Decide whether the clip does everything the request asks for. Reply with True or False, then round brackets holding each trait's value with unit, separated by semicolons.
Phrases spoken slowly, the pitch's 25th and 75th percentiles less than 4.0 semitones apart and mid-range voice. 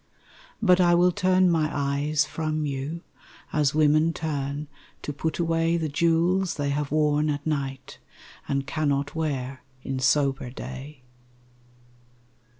True (130 wpm; 2.7 semitones; 150 Hz)